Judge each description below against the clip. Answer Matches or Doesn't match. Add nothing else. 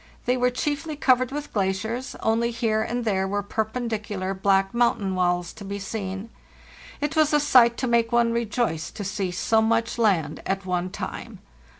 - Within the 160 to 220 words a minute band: Matches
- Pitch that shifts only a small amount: Doesn't match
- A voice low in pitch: Doesn't match